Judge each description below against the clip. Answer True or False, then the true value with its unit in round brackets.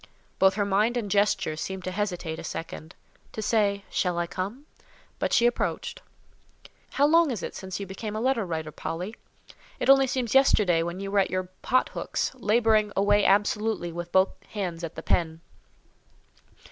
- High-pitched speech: True (200 Hz)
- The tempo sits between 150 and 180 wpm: True (170 wpm)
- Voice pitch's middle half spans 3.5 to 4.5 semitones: True (3.9 semitones)